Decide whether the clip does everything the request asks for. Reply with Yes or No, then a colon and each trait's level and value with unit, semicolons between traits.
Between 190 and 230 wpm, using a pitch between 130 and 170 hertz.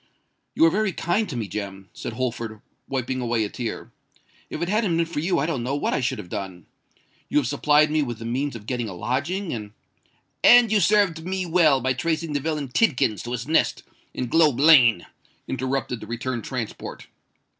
Yes: average, 200 wpm; low, 135 Hz